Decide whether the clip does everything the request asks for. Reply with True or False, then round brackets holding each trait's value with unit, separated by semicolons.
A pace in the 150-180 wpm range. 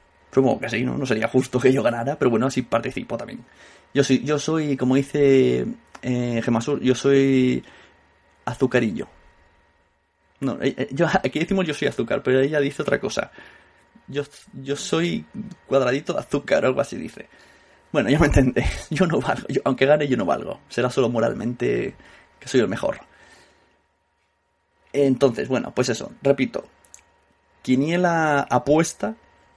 True (155 wpm)